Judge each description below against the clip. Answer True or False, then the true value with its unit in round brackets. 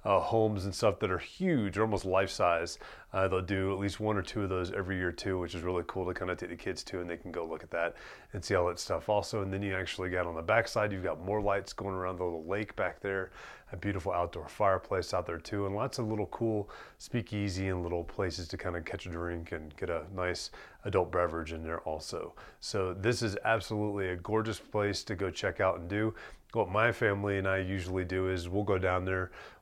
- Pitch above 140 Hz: False (95 Hz)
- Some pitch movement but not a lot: False (2.3 semitones)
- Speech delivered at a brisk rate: True (245 wpm)